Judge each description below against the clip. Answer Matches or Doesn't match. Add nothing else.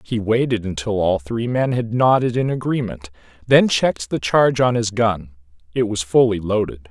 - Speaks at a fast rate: Doesn't match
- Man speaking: Matches